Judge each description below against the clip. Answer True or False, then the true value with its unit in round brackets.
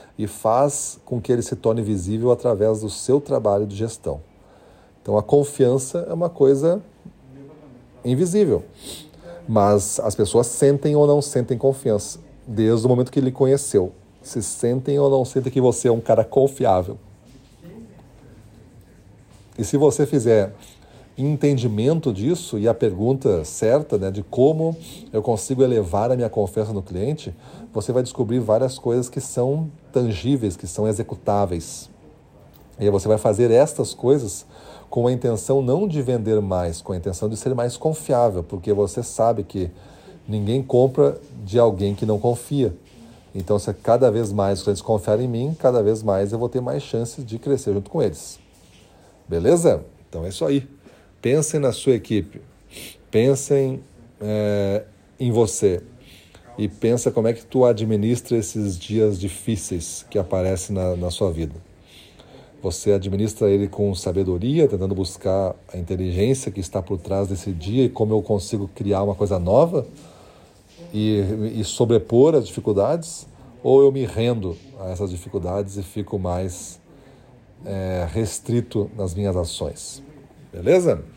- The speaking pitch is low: True (110 Hz)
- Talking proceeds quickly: False (150 wpm)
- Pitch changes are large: False (4.6 semitones)